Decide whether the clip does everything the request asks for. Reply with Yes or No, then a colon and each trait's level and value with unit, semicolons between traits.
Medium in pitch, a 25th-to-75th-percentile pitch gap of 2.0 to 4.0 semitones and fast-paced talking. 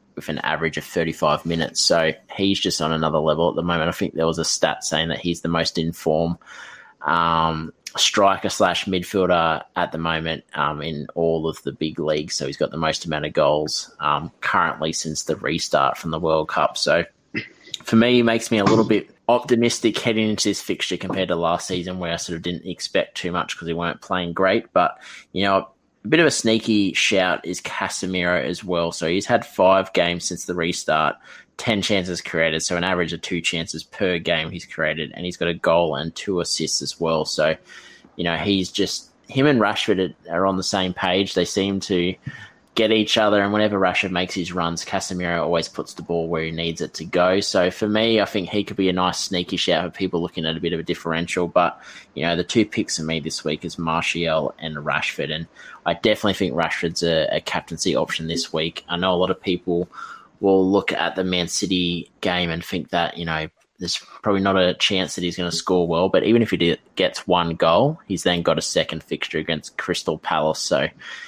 No: very low, 90 Hz; average, 2.7 semitones; fast, 220 wpm